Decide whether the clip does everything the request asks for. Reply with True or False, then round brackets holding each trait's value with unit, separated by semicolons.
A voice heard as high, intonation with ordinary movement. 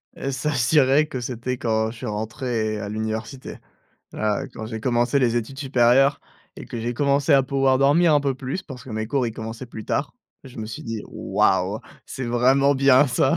False (125 Hz; 3.4 semitones)